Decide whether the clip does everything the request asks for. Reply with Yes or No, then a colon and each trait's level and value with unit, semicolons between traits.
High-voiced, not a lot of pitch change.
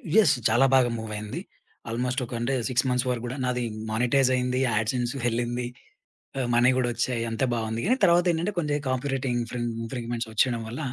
No: low, 125 Hz; narrow, 1.9 semitones